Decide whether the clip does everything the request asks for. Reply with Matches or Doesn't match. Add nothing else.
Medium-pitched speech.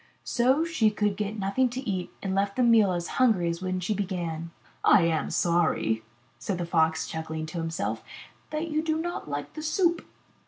Doesn't match